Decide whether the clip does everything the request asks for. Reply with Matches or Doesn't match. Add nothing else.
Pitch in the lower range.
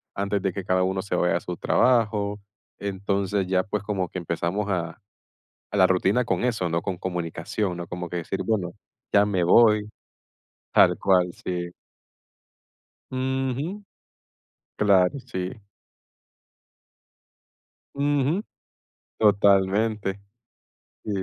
Matches